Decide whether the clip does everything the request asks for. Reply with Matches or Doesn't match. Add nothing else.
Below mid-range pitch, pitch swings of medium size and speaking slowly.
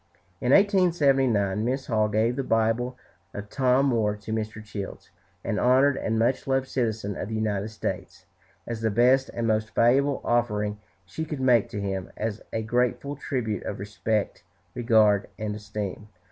Doesn't match